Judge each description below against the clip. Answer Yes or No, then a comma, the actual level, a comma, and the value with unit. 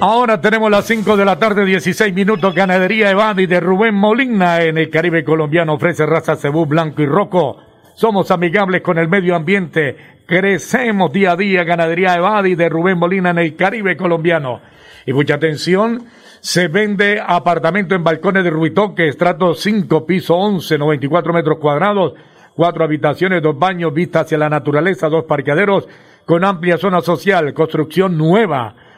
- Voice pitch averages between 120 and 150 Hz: No, medium, 175 Hz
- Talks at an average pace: Yes, average, 160 wpm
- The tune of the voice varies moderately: Yes, average, 3.5 semitones